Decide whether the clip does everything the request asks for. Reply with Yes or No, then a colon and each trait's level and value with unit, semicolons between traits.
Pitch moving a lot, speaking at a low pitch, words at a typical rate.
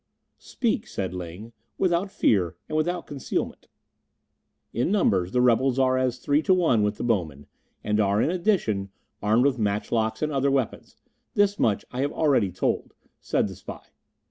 Yes: wide, 6.9 semitones; low, 125 Hz; average, 165 wpm